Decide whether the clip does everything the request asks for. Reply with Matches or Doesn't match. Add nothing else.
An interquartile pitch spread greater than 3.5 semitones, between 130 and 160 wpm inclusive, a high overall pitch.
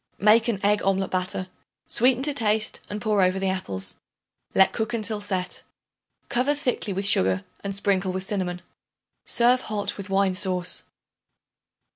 Doesn't match